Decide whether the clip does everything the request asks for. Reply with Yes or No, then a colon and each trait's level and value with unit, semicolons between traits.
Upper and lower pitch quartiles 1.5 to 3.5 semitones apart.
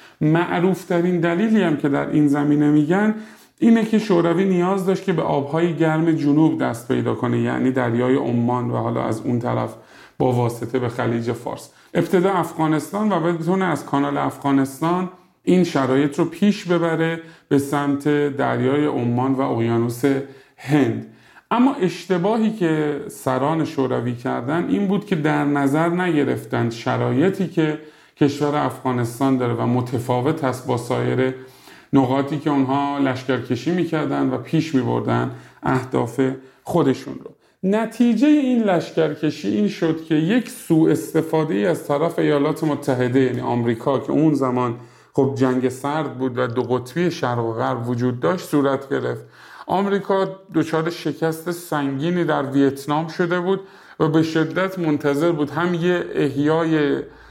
No: average, 4.7 semitones